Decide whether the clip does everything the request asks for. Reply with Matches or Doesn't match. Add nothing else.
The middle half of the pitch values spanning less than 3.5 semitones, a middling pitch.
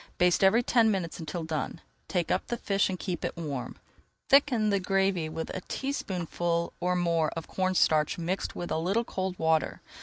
Matches